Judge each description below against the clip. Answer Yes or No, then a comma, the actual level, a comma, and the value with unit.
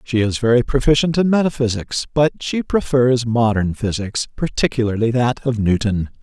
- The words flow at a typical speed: Yes, average, 145 wpm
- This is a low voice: Yes, low, 120 Hz